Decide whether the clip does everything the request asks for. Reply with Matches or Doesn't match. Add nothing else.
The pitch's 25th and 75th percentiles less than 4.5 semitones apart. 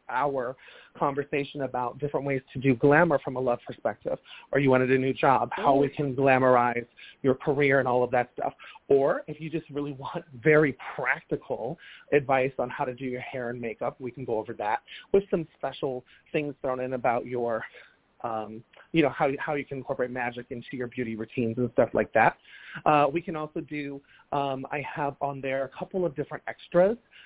Matches